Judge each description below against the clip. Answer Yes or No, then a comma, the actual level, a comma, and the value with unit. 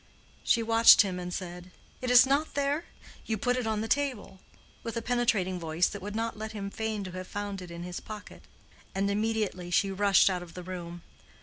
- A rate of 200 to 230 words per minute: Yes, fast, 205 wpm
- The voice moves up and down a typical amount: Yes, average, 3.9 semitones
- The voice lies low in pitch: No, high, 205 Hz